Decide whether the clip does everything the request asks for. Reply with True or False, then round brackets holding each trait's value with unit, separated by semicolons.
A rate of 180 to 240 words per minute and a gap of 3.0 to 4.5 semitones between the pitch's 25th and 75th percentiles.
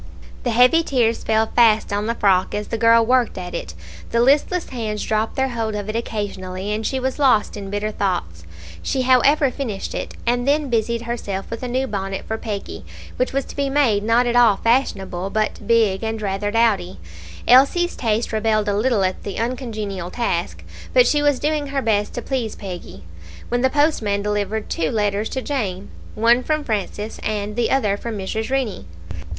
True (190 wpm; 3.6 semitones)